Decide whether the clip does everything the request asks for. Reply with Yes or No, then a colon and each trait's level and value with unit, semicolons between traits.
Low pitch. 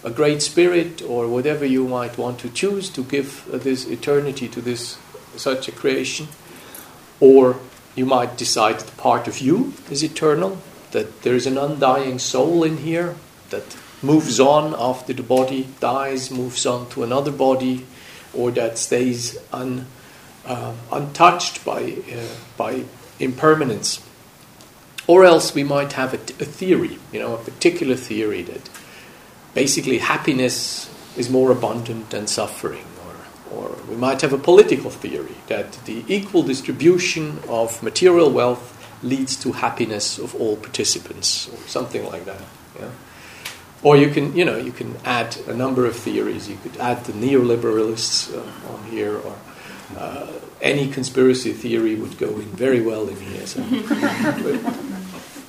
Yes: low, 130 Hz